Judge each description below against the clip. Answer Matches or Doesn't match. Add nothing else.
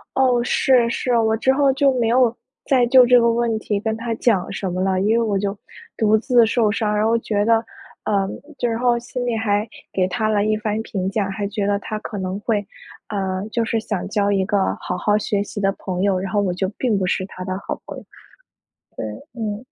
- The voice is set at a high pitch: Matches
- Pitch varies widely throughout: Doesn't match